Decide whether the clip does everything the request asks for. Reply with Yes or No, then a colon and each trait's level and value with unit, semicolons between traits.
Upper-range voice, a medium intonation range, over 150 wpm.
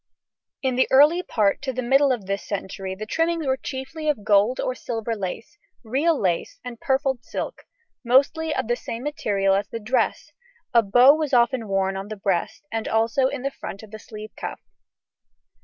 Yes: high, 240 Hz; average, 4.6 semitones; average, 190 wpm